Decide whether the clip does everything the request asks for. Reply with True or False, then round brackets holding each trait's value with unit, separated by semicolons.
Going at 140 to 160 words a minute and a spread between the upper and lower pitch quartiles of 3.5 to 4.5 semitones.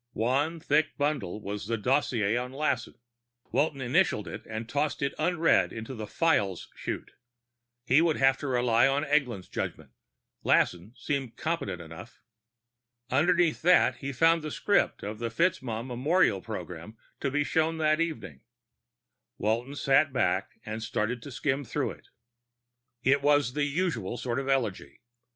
False (150 wpm; 5.1 semitones)